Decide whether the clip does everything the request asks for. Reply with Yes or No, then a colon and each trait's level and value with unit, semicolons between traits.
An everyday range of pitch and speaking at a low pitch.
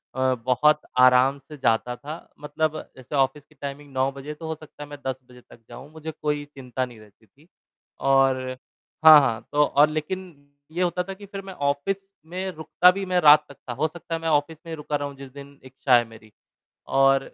No: average, 3.1 semitones; medium, 145 Hz